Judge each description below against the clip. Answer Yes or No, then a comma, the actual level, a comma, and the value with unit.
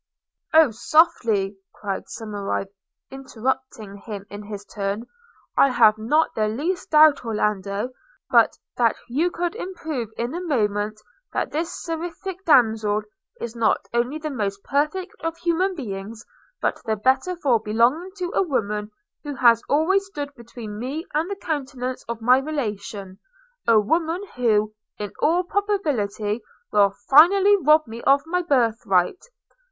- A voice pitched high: Yes, very high, 250 Hz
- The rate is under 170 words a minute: Yes, average, 145 wpm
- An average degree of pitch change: No, wide, 7.0 semitones